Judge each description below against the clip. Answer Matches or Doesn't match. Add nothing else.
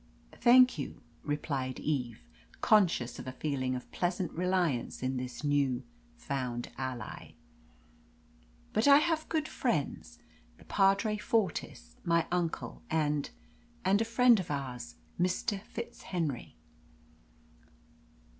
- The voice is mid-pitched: Matches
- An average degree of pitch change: Doesn't match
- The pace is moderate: Doesn't match